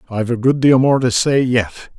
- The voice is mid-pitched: No, low, 125 Hz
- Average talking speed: No, fast, 240 wpm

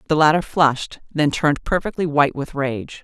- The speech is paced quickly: No, average, 180 wpm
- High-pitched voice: No, medium, 150 Hz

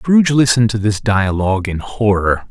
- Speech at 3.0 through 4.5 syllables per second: No, 5.3 syllables/s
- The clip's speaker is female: No, male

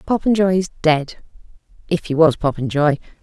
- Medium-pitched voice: Yes, medium, 165 Hz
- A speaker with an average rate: No, slow, 110 wpm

